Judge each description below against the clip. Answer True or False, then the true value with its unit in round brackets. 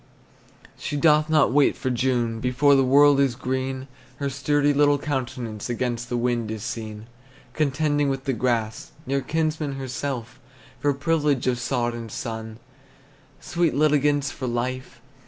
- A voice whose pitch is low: True (130 Hz)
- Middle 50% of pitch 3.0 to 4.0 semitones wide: True (3.3 semitones)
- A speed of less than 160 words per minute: True (150 wpm)